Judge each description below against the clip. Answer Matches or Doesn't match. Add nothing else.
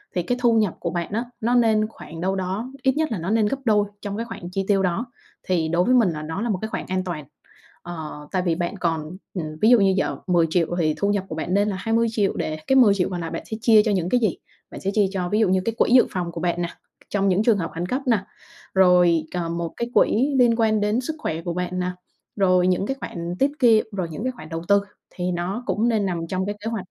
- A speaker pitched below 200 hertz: Matches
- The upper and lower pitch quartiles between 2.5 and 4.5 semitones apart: Matches